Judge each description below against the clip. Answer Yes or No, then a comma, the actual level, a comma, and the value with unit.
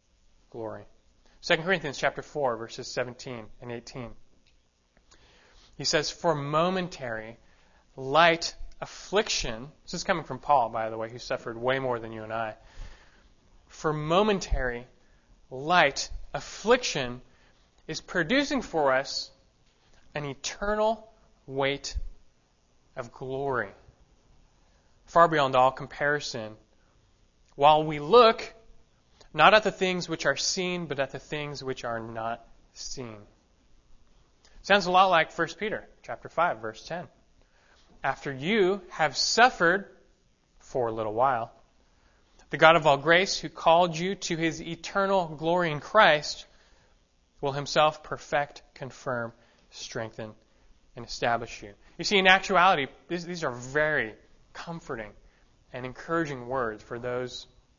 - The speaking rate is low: Yes, slow, 125 wpm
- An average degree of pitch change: No, wide, 6.2 semitones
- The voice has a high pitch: No, medium, 140 Hz